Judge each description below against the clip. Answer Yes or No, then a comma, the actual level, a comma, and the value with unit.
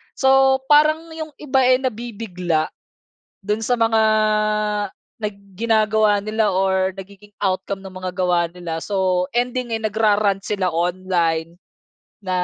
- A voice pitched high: Yes, high, 205 Hz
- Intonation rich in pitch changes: No, average, 3.8 semitones